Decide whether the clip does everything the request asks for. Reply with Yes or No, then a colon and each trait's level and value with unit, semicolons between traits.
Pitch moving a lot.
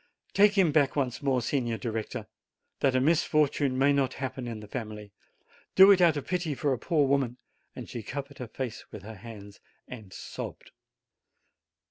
No: average, 4.2 semitones